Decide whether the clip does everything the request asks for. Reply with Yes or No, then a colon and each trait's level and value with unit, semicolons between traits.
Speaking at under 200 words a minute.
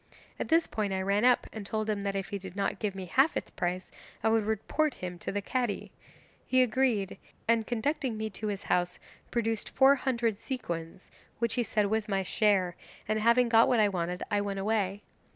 No: fast, 205 wpm